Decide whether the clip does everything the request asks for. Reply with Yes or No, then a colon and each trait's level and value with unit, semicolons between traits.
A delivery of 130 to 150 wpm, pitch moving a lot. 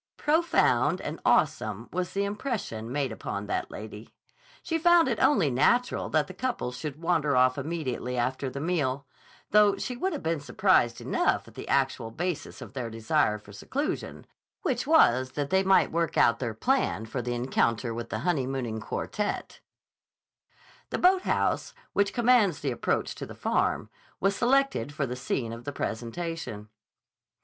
No: average, 160 wpm; wide, 8.9 semitones